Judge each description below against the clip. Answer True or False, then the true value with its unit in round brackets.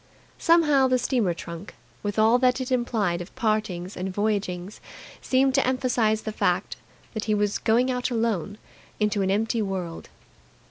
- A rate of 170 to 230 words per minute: False (155 wpm)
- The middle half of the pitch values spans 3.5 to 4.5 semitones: True (4.2 semitones)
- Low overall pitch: False (220 Hz)